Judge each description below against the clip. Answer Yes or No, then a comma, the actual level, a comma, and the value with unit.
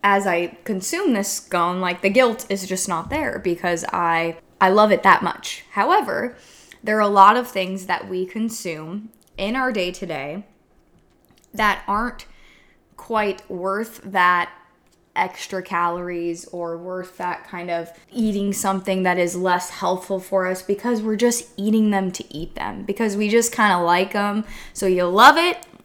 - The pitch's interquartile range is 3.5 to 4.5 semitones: No, average, 3.0 semitones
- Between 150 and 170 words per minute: Yes, average, 165 wpm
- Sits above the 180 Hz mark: Yes, high, 190 Hz